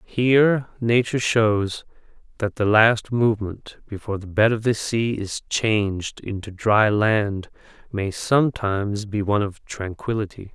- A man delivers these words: Yes, male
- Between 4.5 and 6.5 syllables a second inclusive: No, 4.3 syllables/s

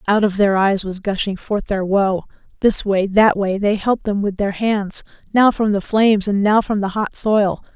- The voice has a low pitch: No, high, 205 Hz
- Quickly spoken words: Yes, fast, 225 wpm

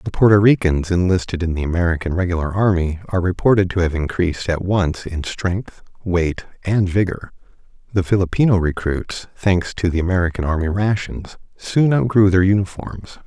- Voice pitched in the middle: No, very low, 90 Hz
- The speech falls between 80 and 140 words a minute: No, average, 155 wpm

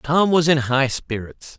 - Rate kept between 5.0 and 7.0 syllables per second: No, 3.9 syllables/s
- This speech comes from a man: Yes, male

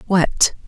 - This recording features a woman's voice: Yes, female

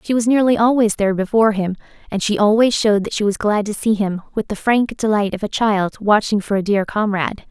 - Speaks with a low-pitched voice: No, high, 210 Hz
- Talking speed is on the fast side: Yes, fast, 240 wpm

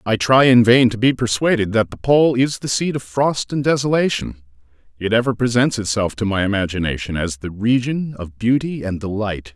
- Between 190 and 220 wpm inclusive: Yes, average, 195 wpm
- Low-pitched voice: Yes, low, 115 Hz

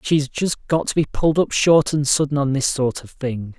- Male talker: Yes, male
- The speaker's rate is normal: No, fast, 250 wpm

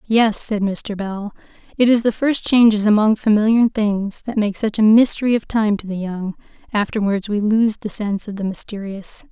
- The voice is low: No, high, 210 Hz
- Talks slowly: No, average, 195 wpm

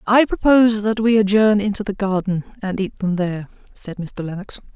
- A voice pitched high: Yes, high, 200 Hz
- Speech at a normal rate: Yes, average, 190 wpm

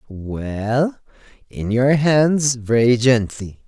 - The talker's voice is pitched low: Yes, low, 125 Hz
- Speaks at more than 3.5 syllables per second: No, 2.7 syllables/s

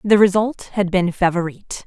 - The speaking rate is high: No, average, 160 wpm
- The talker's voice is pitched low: No, high, 190 Hz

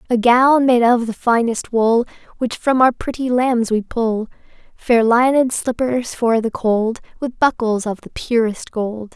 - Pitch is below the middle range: No, high, 235 Hz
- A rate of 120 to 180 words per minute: Yes, average, 170 wpm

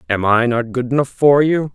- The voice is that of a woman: No, male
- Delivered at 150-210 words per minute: No, fast, 240 wpm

